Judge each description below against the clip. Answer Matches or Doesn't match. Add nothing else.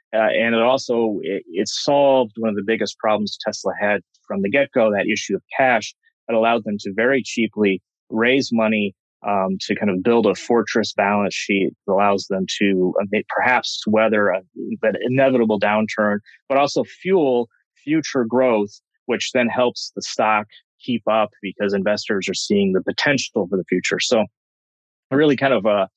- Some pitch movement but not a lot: Matches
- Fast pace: Doesn't match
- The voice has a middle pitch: Doesn't match